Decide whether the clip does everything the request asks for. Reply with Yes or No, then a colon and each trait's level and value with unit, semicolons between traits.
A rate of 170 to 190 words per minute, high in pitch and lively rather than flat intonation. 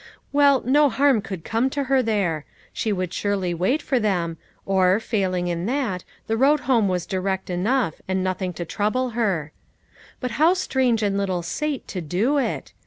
Yes: average, 175 wpm; high, 205 Hz; wide, 6.0 semitones